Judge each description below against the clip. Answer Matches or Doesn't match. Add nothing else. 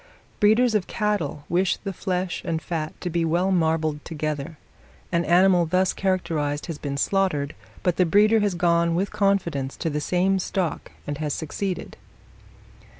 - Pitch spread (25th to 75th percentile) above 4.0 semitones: Doesn't match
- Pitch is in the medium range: Matches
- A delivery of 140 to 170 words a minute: Matches